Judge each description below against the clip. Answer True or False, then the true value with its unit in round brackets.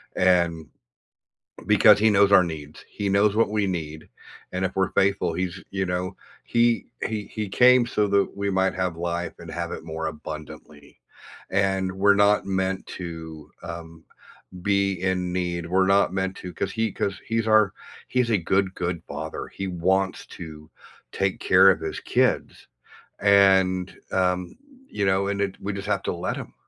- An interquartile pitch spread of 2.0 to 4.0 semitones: True (2.4 semitones)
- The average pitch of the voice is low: True (95 Hz)